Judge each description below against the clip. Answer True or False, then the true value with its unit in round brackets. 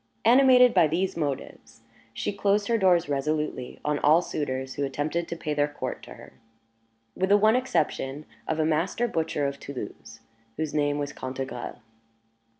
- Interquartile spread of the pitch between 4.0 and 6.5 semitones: True (5.0 semitones)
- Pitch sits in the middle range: True (155 Hz)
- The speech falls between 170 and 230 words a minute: False (160 wpm)